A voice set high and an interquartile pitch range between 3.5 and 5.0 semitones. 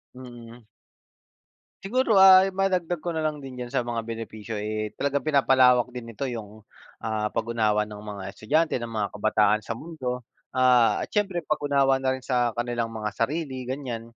No: low, 125 Hz; average, 4.1 semitones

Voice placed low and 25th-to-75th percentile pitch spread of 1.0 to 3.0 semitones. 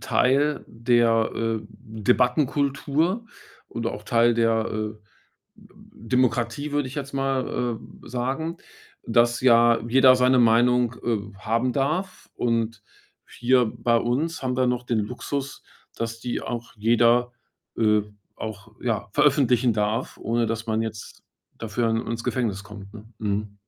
Yes: low, 120 Hz; narrow, 2.4 semitones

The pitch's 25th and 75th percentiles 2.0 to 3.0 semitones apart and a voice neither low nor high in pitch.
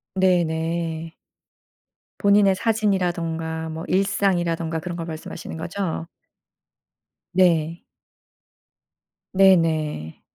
Yes: average, 2.7 semitones; medium, 170 Hz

